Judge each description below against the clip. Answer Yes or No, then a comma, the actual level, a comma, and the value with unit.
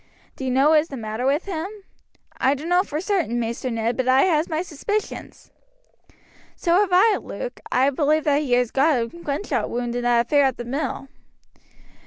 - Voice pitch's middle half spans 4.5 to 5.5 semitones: Yes, average, 5.0 semitones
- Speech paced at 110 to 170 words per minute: No, average, 185 wpm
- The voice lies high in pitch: Yes, very high, 280 Hz